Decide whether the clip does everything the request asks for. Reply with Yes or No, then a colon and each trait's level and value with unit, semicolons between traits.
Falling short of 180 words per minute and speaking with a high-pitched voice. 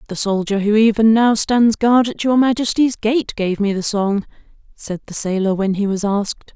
No: average, 200 wpm; high, 215 Hz